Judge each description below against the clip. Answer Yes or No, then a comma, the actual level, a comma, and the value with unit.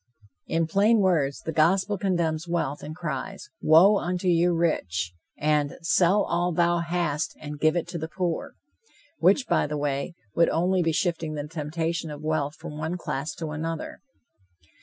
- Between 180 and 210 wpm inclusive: No, average, 165 wpm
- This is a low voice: No, medium, 165 Hz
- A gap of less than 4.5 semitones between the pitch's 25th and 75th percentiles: Yes, narrow, 2.6 semitones